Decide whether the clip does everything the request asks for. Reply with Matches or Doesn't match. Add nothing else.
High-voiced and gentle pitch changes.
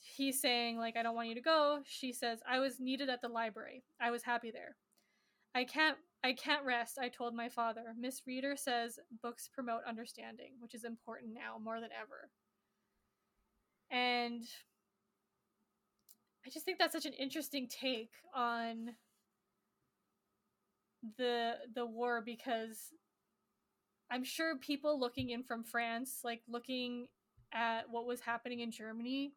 Matches